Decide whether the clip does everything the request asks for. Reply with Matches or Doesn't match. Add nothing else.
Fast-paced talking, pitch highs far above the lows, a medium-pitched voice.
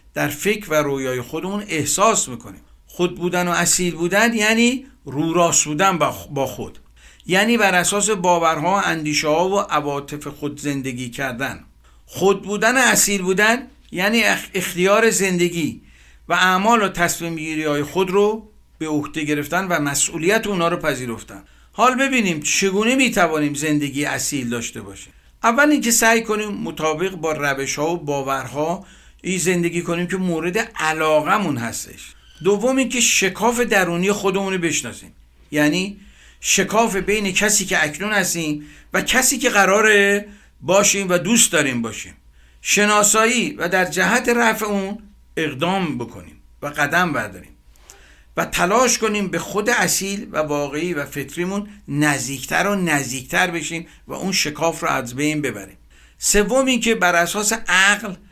Doesn't match